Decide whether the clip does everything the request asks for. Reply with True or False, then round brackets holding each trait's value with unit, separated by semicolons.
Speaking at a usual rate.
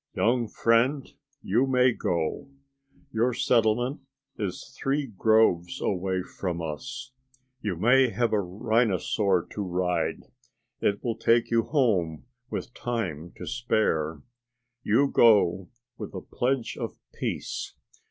False (120 wpm)